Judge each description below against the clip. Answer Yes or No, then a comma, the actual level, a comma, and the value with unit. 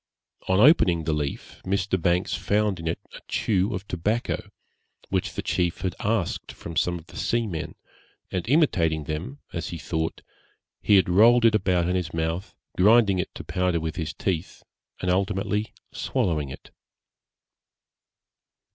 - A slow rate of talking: No, average, 155 wpm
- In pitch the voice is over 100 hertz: No, very low, 90 Hz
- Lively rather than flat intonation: No, average, 3.8 semitones